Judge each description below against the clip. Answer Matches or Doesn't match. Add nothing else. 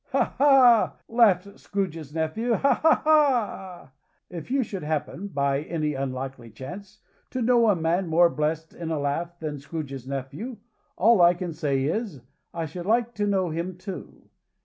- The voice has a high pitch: Doesn't match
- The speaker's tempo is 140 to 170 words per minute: Matches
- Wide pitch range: Matches